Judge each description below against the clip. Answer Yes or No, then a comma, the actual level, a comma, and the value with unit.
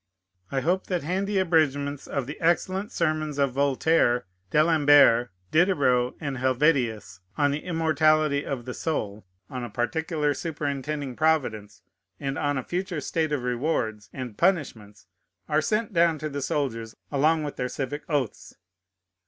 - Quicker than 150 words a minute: No, average, 145 wpm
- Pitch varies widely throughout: No, average, 4.1 semitones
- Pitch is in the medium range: Yes, medium, 145 Hz